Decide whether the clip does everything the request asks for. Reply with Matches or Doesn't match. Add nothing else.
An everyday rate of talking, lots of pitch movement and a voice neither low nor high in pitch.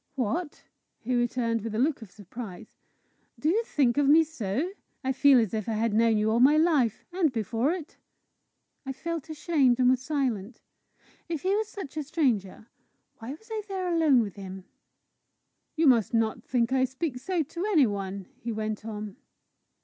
Doesn't match